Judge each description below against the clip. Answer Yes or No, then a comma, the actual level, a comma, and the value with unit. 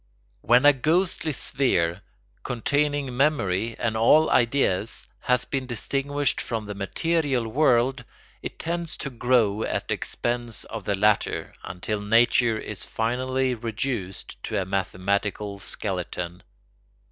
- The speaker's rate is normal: No, slow, 125 wpm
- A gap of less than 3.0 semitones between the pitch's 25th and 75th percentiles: No, average, 4.8 semitones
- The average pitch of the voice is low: Yes, low, 120 Hz